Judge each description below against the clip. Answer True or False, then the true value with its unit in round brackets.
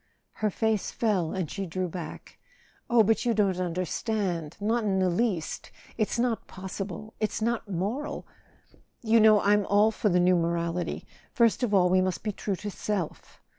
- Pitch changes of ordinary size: True (3.3 semitones)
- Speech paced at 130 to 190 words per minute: True (165 wpm)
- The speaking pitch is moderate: False (200 Hz)